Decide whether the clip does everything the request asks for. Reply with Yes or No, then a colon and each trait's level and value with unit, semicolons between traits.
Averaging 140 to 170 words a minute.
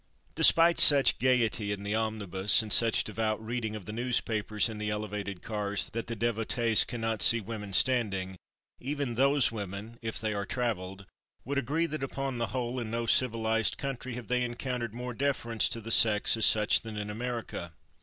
No: average, 180 wpm